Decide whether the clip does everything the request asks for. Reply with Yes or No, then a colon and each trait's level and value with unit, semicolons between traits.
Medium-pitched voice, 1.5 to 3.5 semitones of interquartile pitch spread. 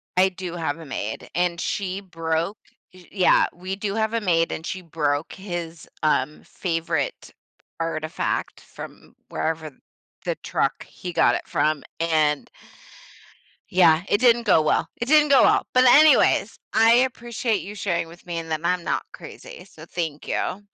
No: medium, 175 Hz; average, 4.1 semitones